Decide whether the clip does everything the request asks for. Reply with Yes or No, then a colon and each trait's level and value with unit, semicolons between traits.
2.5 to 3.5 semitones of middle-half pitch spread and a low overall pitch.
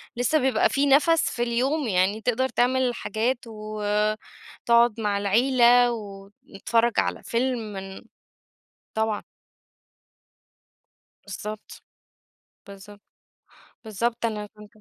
No: average, 2.9 semitones; high, 225 Hz